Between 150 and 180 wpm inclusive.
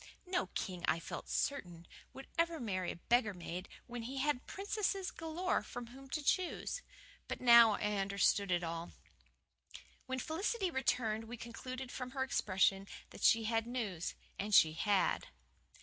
Yes: average, 155 wpm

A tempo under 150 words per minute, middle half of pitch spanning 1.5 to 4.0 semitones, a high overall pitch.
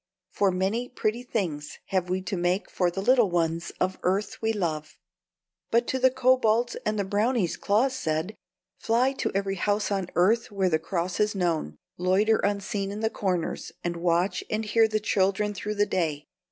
No: average, 180 wpm; average, 3.4 semitones; high, 200 Hz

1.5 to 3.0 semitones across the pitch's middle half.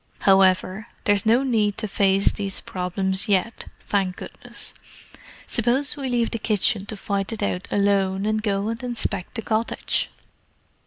Yes: average, 2.7 semitones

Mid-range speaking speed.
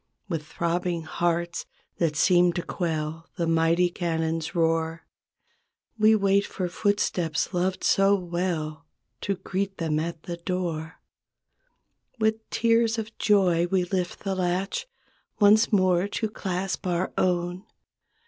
No: slow, 125 wpm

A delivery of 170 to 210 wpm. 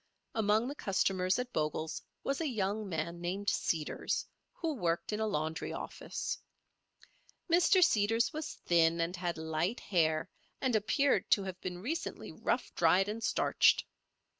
No: average, 145 wpm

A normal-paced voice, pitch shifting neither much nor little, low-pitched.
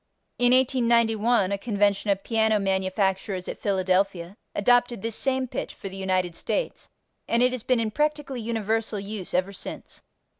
No: average, 155 wpm; average, 3.9 semitones; high, 215 Hz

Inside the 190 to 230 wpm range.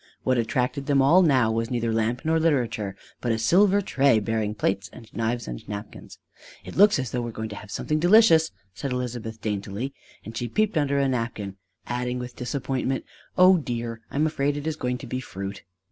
Yes: fast, 205 wpm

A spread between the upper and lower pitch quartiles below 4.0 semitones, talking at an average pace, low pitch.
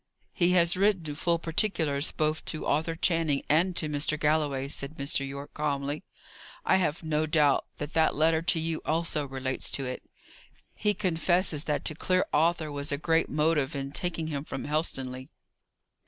No: narrow, 2.6 semitones; average, 170 wpm; medium, 155 Hz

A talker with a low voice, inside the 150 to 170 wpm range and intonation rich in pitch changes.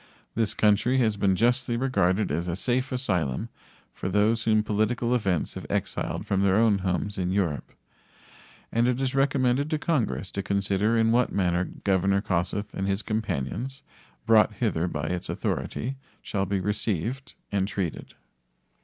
No: low, 105 Hz; average, 155 wpm; average, 4.1 semitones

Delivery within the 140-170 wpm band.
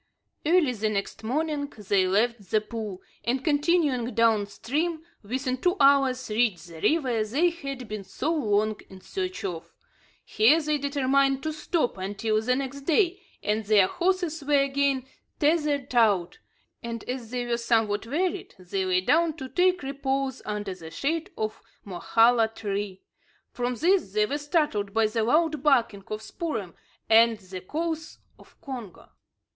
Yes: average, 155 wpm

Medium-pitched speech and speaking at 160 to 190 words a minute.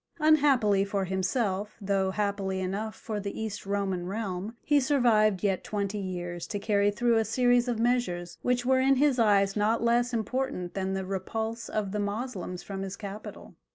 No: high, 210 Hz; average, 175 wpm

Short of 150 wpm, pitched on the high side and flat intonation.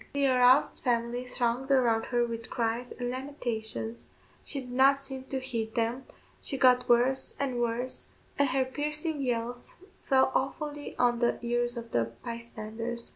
No: average, 155 wpm; high, 245 Hz; narrow, 2.1 semitones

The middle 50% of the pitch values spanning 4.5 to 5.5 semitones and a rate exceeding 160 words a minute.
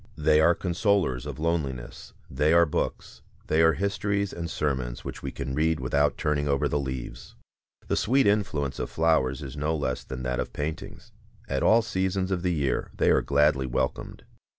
No: average, 4.1 semitones; average, 180 wpm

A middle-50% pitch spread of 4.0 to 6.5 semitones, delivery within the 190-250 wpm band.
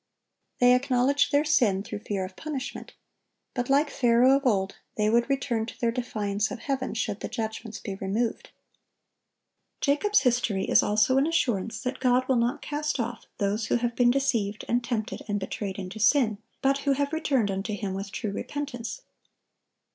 No: average, 4.3 semitones; average, 175 wpm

